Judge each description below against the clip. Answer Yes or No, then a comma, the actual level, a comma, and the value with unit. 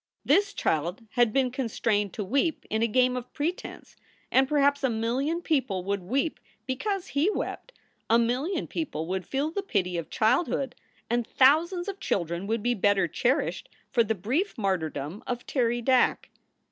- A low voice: No, high, 245 Hz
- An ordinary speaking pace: Yes, average, 170 wpm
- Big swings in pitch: Yes, wide, 5.8 semitones